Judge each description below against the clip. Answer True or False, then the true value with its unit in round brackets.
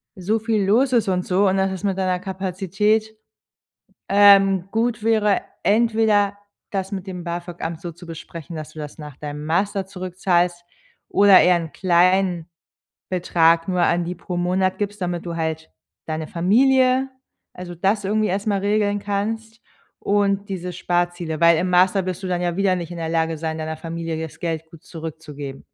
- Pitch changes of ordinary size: True (3.2 semitones)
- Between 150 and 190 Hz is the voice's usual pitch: True (185 Hz)